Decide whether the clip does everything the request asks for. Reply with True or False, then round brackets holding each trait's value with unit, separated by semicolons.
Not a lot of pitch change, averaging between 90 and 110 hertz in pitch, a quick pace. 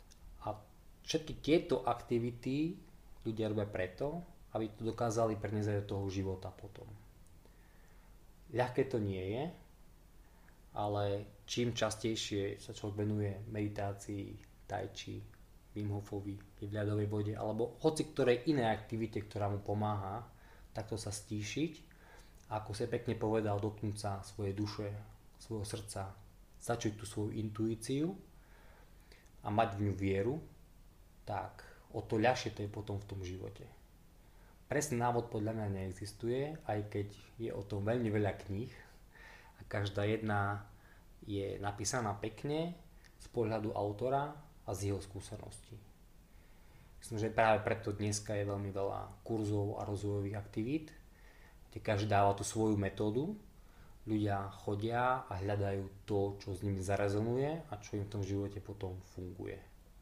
False (2.3 semitones; 105 Hz; 130 wpm)